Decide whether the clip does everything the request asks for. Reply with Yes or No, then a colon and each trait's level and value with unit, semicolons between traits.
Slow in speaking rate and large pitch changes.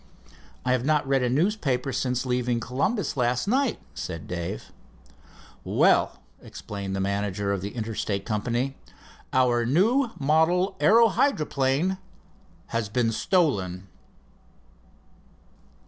Yes: slow, 110 wpm; wide, 6.9 semitones